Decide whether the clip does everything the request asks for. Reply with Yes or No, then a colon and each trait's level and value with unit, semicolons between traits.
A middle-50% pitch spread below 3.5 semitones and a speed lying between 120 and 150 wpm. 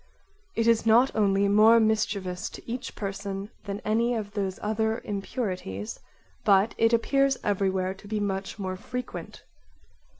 Yes: narrow, 2.6 semitones; average, 140 wpm